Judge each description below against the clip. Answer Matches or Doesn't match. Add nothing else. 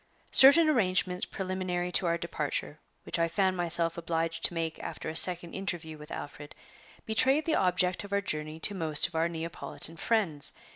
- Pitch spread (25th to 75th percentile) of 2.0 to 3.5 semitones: Matches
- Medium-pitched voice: Matches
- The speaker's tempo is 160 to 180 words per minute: Matches